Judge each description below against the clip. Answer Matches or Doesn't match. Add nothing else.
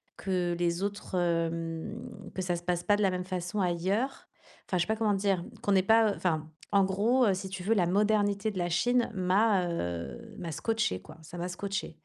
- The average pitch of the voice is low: Doesn't match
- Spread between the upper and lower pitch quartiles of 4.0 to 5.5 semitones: Doesn't match